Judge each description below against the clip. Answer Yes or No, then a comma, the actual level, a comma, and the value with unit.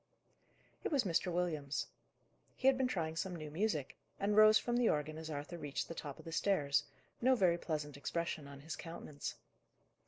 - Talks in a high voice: No, medium, 165 Hz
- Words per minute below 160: No, average, 185 wpm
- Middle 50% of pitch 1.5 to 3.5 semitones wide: No, average, 5.1 semitones